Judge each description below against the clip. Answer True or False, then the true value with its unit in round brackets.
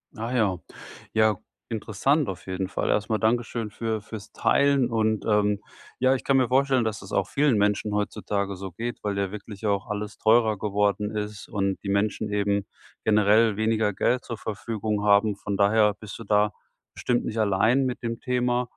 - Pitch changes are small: True (2.2 semitones)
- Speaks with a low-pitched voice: True (105 Hz)